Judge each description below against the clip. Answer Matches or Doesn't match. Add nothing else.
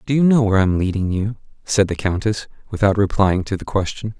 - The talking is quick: Matches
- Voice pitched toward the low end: Matches